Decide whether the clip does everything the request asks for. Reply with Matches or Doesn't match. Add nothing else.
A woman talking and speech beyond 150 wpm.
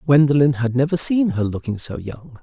Doesn't match